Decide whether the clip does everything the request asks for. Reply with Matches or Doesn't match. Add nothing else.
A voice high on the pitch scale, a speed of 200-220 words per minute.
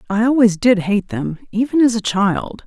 Matches